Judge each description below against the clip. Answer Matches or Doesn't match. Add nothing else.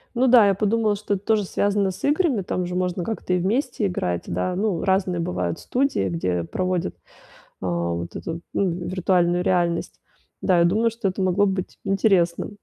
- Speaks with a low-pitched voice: Doesn't match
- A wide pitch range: Doesn't match